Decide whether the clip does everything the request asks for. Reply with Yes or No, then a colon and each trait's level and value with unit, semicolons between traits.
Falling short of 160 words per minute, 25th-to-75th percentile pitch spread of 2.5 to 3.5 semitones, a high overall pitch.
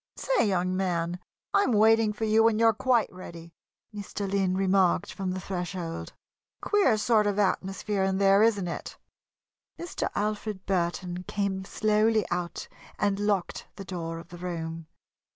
Yes: average, 150 wpm; average, 2.9 semitones; high, 195 Hz